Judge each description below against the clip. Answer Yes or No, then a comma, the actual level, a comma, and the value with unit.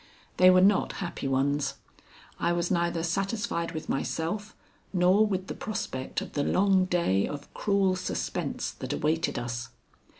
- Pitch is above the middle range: No, medium, 175 Hz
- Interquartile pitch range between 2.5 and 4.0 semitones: No, average, 4.6 semitones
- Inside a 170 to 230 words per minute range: No, average, 145 wpm